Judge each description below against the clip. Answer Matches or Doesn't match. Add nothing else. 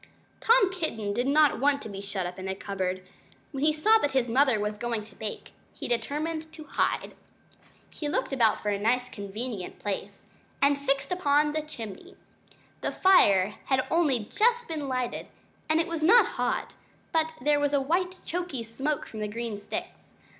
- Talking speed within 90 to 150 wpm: Doesn't match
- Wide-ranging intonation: Matches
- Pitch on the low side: Doesn't match